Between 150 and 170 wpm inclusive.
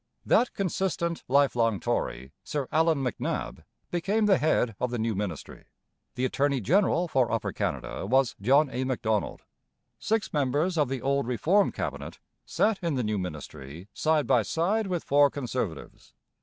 Yes: average, 155 wpm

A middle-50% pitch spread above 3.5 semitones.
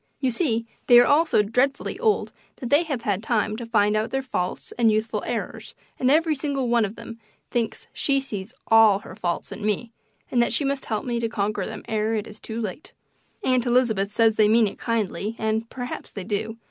No: average, 2.9 semitones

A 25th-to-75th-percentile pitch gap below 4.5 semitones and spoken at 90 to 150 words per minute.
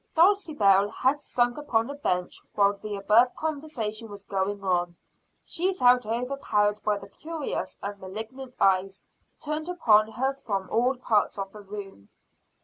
No: average, 5.2 semitones; average, 145 wpm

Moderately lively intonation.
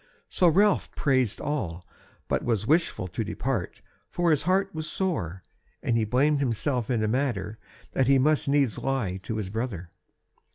No: wide, 5.7 semitones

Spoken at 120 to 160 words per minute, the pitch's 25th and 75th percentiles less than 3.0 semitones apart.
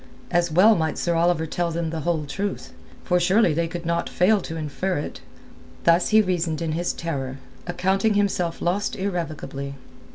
No: average, 170 wpm; narrow, 2.4 semitones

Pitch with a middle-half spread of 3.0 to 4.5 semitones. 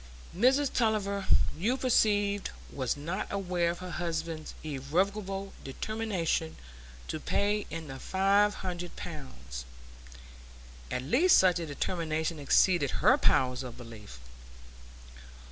No: average, 5.2 semitones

